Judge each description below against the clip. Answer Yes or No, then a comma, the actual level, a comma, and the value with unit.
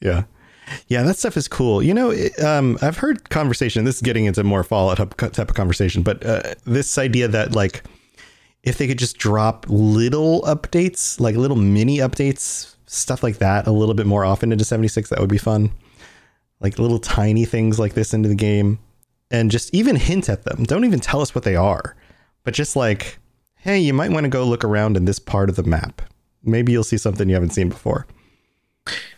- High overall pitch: No, low, 115 Hz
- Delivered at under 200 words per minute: No, fast, 205 wpm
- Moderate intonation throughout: Yes, average, 4.1 semitones